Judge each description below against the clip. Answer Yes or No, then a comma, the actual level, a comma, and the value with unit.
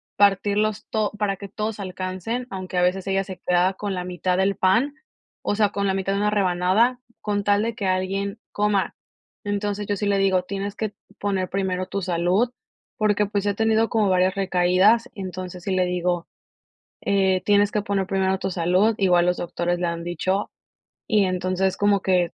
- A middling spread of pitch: No, narrow, 1.9 semitones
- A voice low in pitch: No, high, 195 Hz